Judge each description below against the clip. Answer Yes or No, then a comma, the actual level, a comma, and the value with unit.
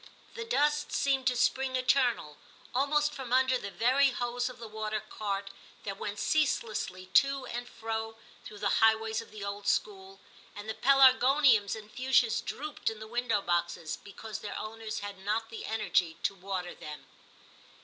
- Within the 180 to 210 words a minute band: No, average, 165 wpm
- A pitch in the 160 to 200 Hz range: No, high, 225 Hz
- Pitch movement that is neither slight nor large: Yes, average, 4.1 semitones